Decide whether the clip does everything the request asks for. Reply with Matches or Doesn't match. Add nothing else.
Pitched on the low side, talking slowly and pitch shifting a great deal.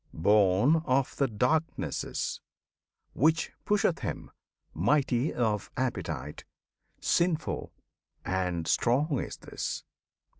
Matches